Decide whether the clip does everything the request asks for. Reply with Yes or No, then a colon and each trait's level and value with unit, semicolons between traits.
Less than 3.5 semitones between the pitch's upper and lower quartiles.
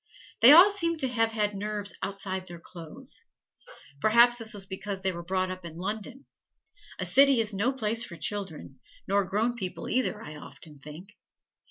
No: average, 3.9 semitones